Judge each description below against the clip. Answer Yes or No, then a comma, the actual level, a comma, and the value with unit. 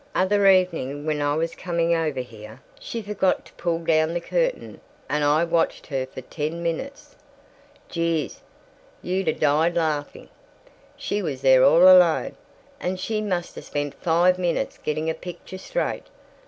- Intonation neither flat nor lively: Yes, average, 3.4 semitones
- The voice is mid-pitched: Yes, medium, 165 Hz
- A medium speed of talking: Yes, average, 155 wpm